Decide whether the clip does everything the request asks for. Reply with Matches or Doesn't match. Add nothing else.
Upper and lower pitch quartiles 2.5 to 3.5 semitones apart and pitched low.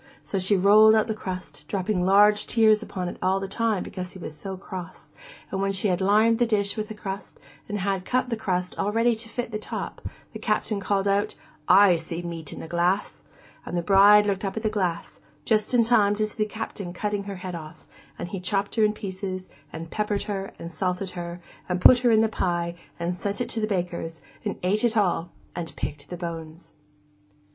Doesn't match